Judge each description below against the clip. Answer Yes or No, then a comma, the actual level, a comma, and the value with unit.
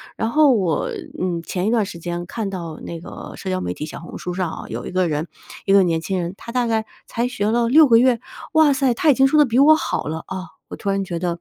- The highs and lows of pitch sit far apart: Yes, wide, 5.8 semitones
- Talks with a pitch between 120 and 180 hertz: No, high, 195 Hz